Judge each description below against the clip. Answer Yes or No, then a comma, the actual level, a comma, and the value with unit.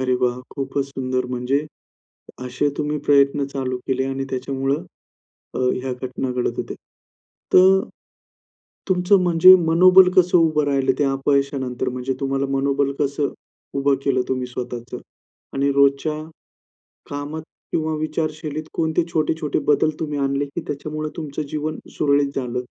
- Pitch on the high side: No, medium, 140 Hz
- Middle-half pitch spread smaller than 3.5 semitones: Yes, narrow, 2.6 semitones